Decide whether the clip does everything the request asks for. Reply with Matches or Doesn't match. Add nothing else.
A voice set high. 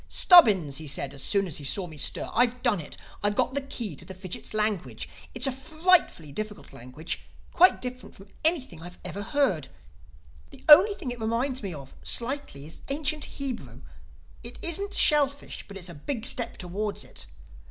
Matches